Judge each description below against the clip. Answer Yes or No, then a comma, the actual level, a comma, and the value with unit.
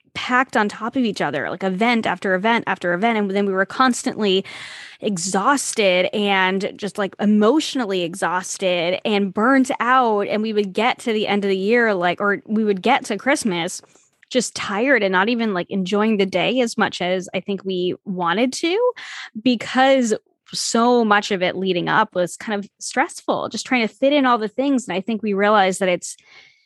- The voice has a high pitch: Yes, high, 210 Hz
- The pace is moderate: Yes, average, 195 wpm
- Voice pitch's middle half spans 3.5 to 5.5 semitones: Yes, average, 4.5 semitones